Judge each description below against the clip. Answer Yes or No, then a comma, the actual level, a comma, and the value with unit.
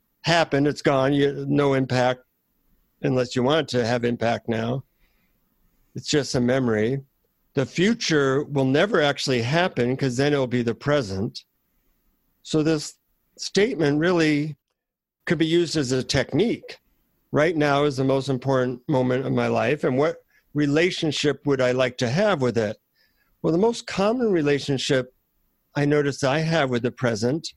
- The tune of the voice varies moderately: Yes, average, 3.5 semitones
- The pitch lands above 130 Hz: Yes, medium, 140 Hz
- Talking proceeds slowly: No, average, 155 wpm